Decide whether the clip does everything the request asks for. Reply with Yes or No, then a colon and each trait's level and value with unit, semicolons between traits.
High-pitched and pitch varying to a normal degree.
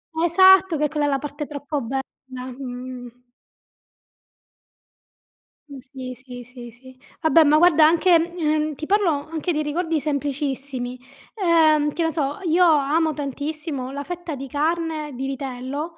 Yes: very high, 295 Hz; average, 3.3 semitones